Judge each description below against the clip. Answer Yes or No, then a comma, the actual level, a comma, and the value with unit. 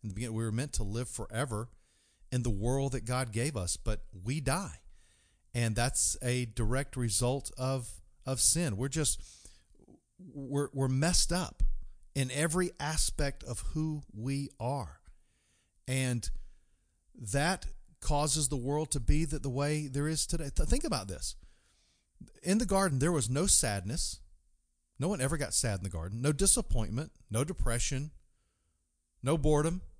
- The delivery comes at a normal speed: Yes, average, 150 wpm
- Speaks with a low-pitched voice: Yes, low, 125 Hz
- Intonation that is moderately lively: No, wide, 6.2 semitones